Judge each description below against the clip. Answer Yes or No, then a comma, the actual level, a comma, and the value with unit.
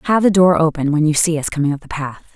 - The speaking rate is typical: No, fast, 305 wpm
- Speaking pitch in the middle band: Yes, medium, 160 Hz